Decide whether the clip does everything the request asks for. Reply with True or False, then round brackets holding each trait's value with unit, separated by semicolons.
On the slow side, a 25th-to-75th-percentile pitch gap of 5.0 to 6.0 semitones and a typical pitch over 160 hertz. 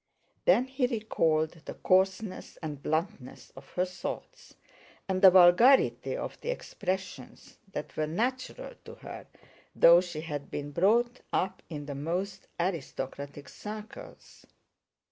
True (125 wpm; 5.6 semitones; 185 Hz)